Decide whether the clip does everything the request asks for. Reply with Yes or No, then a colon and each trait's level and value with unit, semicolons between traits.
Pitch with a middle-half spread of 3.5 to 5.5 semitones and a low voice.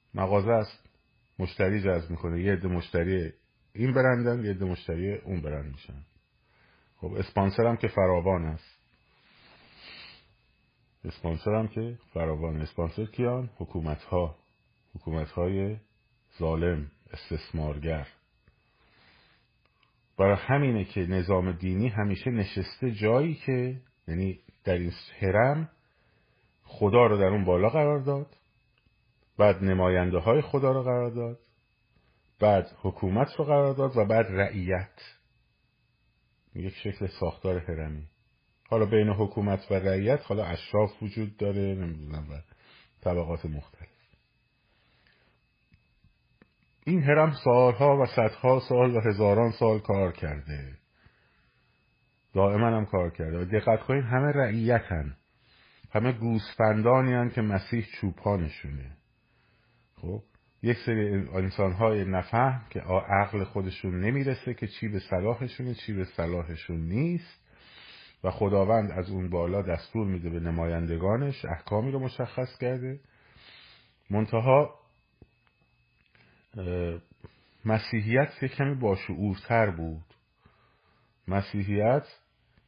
Yes: average, 4.7 semitones; low, 105 Hz